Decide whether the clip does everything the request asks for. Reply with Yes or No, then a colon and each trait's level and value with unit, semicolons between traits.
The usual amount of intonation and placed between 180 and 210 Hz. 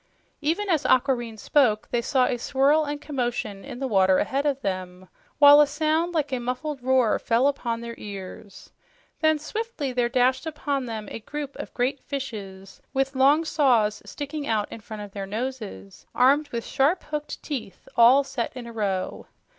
No: average, 4.6 semitones; very high, 260 Hz